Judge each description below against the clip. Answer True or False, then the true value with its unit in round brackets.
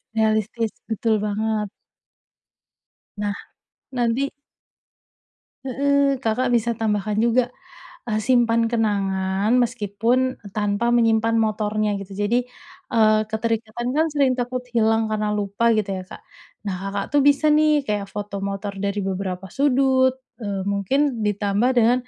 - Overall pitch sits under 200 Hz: False (220 Hz)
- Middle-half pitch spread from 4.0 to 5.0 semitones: False (3.3 semitones)